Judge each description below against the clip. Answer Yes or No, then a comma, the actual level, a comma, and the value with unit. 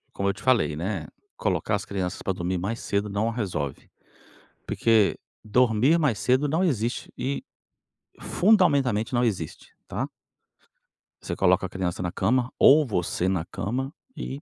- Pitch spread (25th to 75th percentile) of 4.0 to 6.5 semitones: Yes, wide, 5.6 semitones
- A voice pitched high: No, low, 110 Hz